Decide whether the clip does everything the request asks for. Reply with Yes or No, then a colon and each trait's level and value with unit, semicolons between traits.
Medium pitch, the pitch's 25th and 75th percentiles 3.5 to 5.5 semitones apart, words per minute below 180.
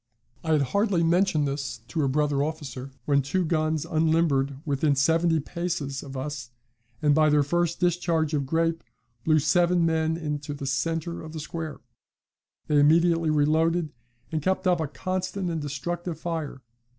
No: medium, 155 Hz; average, 2.7 semitones; average, 160 wpm